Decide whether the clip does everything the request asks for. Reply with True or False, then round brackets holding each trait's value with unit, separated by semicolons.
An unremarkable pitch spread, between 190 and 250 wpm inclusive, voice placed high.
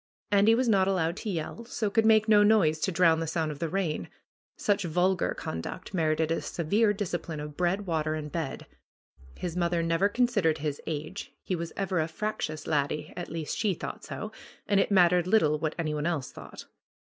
False (4.2 semitones; 200 wpm; 170 Hz)